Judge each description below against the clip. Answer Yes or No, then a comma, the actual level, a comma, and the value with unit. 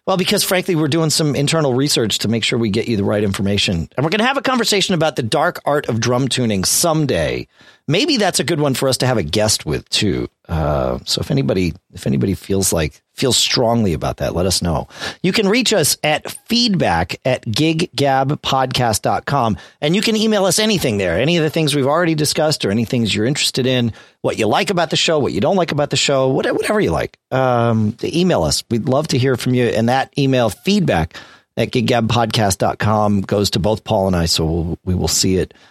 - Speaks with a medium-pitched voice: No, low, 130 Hz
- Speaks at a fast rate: Yes, fast, 220 wpm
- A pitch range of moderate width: No, wide, 7.0 semitones